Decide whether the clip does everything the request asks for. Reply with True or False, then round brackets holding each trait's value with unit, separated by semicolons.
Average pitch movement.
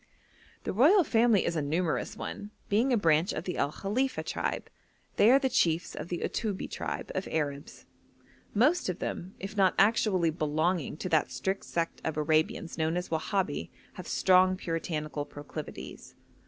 True (4.5 semitones)